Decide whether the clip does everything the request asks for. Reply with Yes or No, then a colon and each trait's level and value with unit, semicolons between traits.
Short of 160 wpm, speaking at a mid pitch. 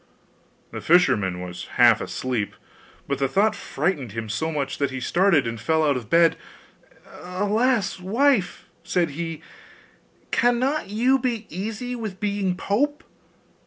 Yes: slow, 135 wpm; medium, 180 Hz